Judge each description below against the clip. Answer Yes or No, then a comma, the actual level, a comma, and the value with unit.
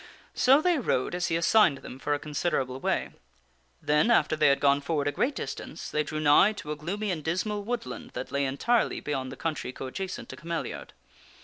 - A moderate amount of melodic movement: No, wide, 6.4 semitones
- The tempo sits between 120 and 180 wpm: No, average, 200 wpm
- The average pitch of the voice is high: No, medium, 155 Hz